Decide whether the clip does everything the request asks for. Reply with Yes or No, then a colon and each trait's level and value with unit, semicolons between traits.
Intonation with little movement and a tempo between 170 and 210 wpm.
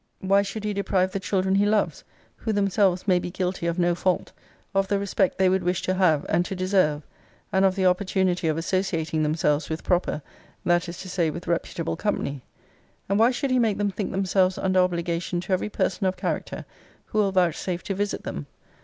Yes: narrow, 2.2 semitones; fast, 205 wpm